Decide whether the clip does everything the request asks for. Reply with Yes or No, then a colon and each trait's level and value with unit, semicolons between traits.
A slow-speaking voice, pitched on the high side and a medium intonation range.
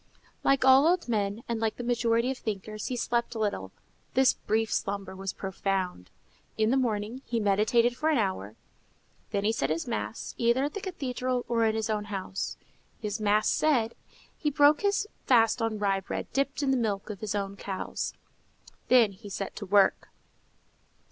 No: average, 180 wpm; high, 220 Hz; average, 3.8 semitones